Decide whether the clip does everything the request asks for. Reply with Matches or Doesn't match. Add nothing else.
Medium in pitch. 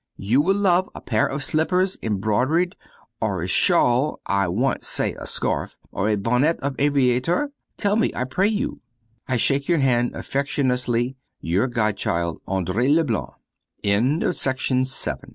Doesn't match